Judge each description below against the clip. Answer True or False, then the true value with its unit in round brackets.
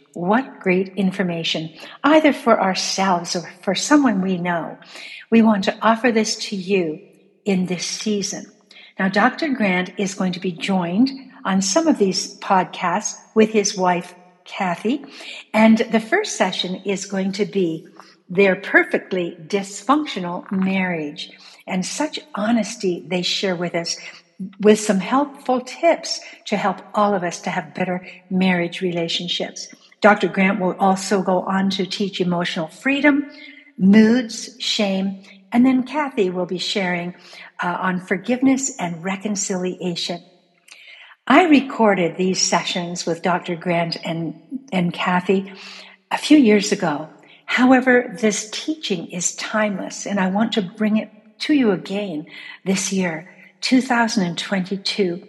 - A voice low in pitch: False (195 Hz)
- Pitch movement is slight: False (3.6 semitones)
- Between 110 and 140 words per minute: True (135 wpm)